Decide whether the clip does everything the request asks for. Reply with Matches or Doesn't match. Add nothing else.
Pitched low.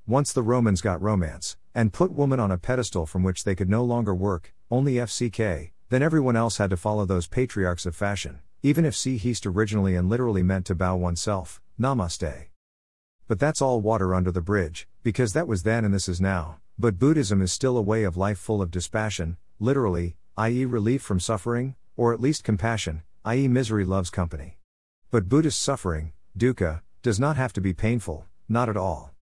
Matches